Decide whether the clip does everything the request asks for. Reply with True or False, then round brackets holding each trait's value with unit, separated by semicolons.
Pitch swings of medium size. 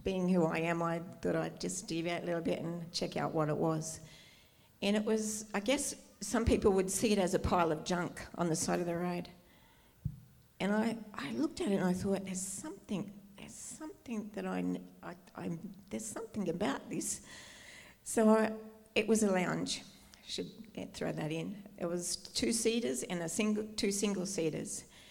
True (4.2 semitones)